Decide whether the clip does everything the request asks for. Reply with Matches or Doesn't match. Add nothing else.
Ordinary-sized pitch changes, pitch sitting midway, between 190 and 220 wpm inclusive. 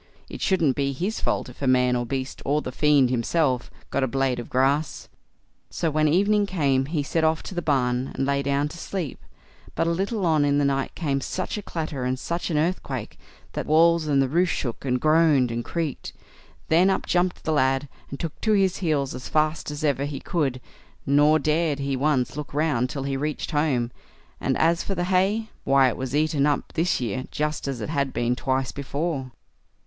Matches